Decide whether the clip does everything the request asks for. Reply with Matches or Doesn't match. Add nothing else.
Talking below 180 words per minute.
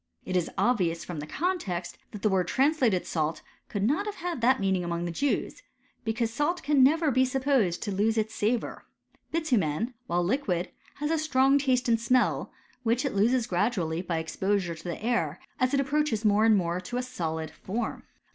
Doesn't match